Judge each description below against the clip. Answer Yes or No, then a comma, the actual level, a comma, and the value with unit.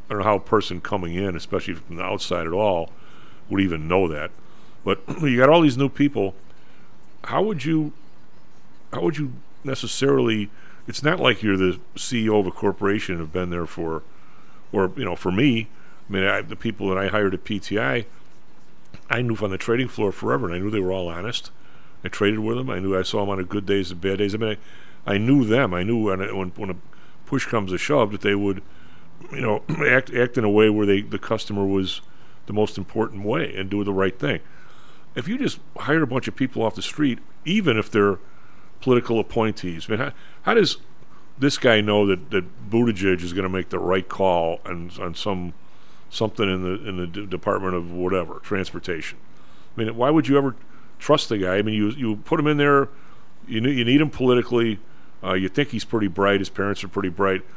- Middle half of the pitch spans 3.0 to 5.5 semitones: Yes, average, 3.8 semitones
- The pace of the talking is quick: Yes, fast, 220 wpm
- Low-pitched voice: Yes, low, 105 Hz